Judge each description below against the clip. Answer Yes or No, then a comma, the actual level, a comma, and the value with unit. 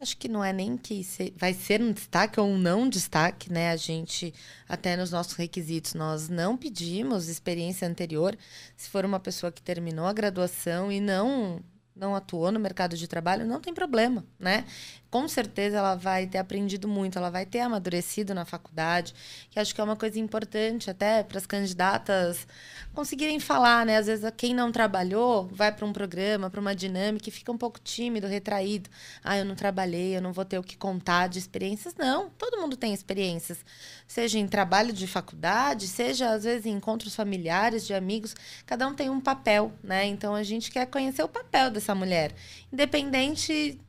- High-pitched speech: Yes, high, 200 Hz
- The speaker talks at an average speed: No, fast, 190 wpm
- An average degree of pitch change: Yes, average, 3.8 semitones